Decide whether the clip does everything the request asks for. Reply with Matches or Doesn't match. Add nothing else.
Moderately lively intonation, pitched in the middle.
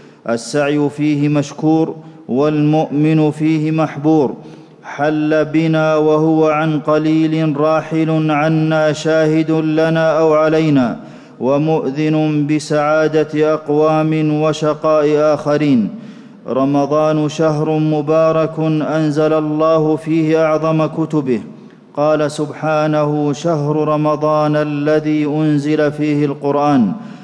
Doesn't match